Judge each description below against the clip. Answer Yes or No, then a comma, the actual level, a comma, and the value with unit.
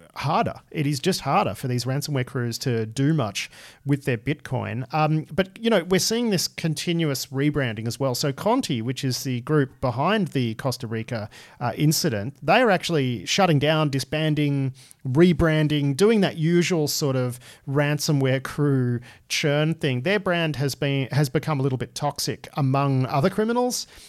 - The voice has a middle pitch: Yes, medium, 145 Hz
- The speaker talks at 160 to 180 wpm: Yes, average, 165 wpm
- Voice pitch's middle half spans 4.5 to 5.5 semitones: No, average, 3.5 semitones